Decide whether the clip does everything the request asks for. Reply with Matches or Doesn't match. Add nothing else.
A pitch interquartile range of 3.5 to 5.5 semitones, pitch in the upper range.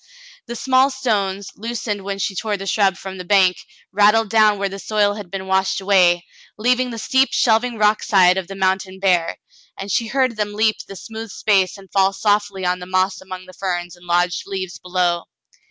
Doesn't match